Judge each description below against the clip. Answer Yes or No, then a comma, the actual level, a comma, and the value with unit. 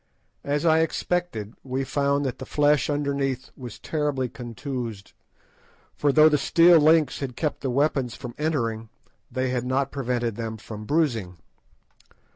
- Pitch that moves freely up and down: No, average, 3.6 semitones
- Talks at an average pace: Yes, average, 145 wpm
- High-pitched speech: No, low, 135 Hz